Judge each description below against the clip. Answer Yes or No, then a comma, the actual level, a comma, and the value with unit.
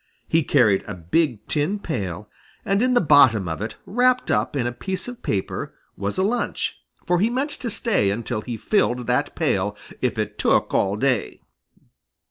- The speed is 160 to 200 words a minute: Yes, average, 180 wpm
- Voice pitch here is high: No, medium, 140 Hz